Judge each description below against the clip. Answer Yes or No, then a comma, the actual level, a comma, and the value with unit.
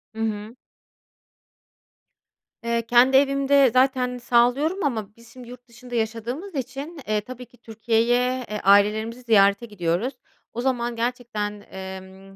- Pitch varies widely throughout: No, average, 2.9 semitones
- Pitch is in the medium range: No, high, 235 Hz